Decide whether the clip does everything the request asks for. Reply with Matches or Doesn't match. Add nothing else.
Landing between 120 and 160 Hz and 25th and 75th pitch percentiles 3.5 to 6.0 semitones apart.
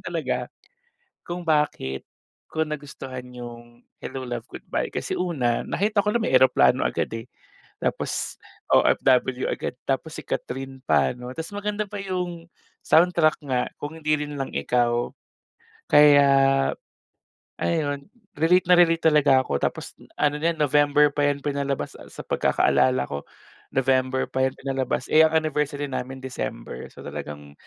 Matches